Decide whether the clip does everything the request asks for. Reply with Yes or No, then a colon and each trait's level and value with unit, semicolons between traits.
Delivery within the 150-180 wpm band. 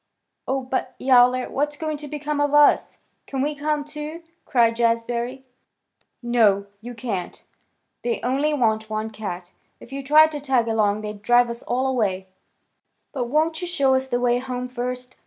Yes: average, 170 wpm